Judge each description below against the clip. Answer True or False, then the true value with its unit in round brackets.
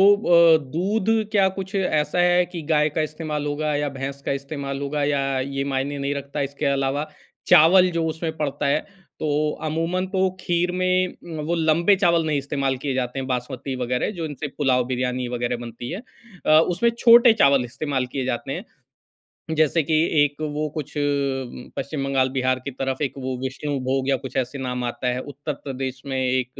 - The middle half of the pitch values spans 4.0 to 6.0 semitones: False (3.5 semitones)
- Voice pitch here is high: False (145 Hz)